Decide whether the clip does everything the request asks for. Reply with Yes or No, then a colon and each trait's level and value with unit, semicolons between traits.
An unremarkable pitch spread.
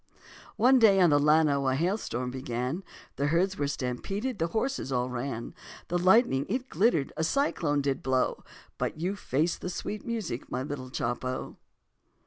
No: wide, 6.9 semitones